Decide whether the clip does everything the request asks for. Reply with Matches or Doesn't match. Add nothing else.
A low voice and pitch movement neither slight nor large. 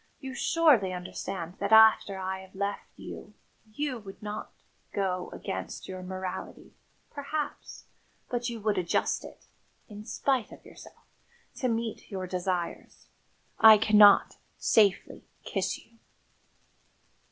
Doesn't match